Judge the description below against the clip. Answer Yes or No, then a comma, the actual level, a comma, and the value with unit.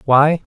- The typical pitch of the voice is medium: Yes, medium, 145 Hz